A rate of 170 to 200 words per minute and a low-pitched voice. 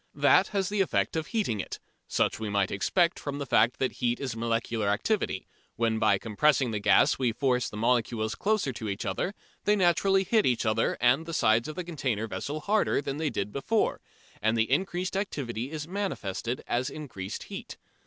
Yes: average, 185 wpm; low, 130 Hz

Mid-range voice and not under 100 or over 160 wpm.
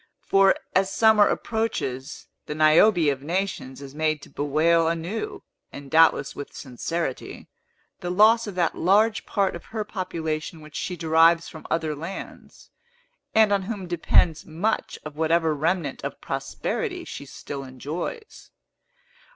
Yes: medium, 165 Hz; average, 140 wpm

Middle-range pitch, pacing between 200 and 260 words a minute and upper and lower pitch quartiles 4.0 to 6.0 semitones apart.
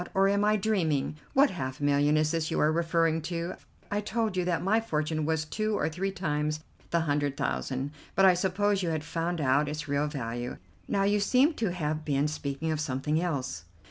Yes: medium, 160 Hz; fast, 205 wpm; average, 4.5 semitones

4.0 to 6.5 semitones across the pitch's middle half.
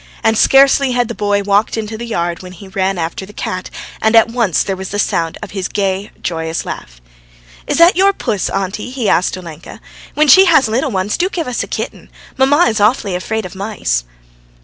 Yes: average, 4.8 semitones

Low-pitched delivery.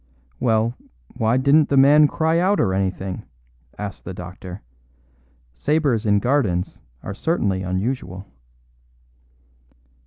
Yes: low, 110 Hz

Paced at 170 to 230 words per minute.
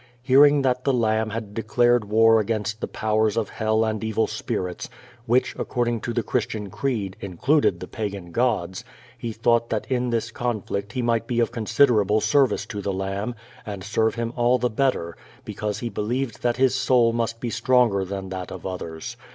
Yes: average, 185 wpm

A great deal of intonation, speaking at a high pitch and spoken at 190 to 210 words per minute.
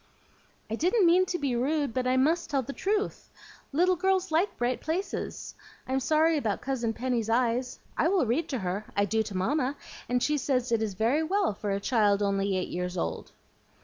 Yes: wide, 6.4 semitones; very high, 255 Hz; average, 200 wpm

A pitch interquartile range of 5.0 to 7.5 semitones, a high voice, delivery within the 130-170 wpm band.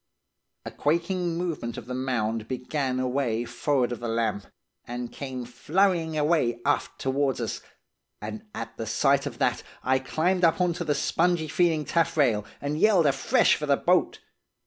No: wide, 5.4 semitones; medium, 140 Hz; average, 165 wpm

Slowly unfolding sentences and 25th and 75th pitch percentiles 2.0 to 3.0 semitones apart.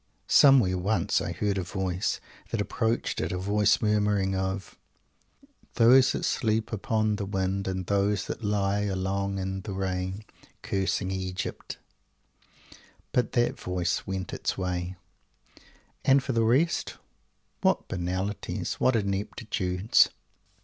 Yes: slow, 130 wpm; narrow, 2.4 semitones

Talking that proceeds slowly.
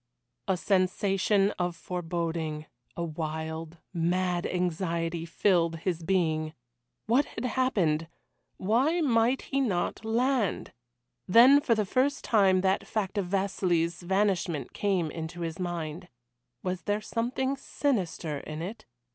Yes: slow, 120 wpm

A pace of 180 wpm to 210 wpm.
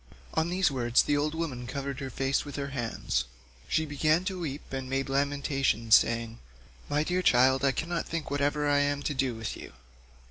Yes: average, 190 wpm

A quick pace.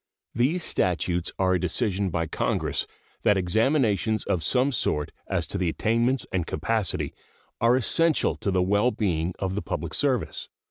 No: average, 150 wpm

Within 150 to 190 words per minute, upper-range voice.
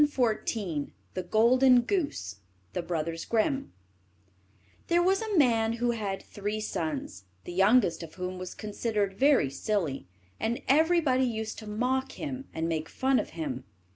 No: average, 140 wpm; high, 215 Hz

